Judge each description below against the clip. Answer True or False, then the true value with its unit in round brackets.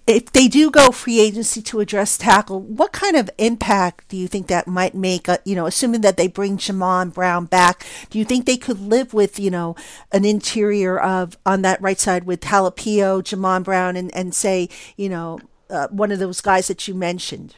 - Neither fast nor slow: False (210 wpm)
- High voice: True (195 Hz)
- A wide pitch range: False (2.8 semitones)